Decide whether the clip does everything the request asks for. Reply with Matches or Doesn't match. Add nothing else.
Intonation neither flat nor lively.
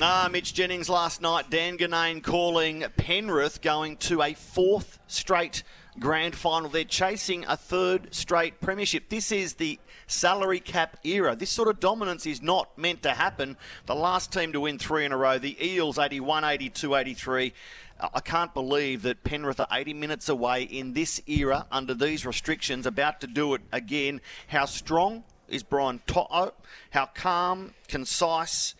Matches